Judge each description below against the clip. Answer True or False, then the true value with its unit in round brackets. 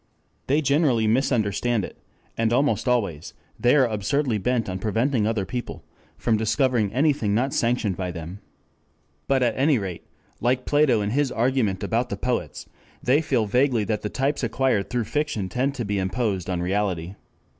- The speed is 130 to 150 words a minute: False (165 wpm)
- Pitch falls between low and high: False (115 Hz)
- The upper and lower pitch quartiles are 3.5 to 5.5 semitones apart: True (4.4 semitones)